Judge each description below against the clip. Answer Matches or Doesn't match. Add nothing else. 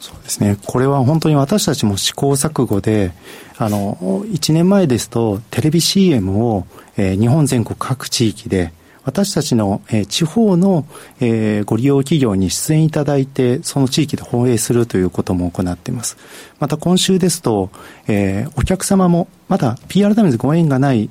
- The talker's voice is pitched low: Matches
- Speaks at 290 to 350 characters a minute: Matches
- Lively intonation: Matches